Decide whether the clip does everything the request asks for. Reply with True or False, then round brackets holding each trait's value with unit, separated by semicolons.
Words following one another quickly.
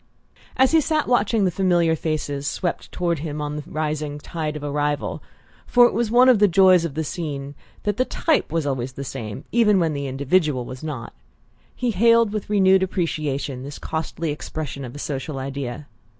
False (190 wpm)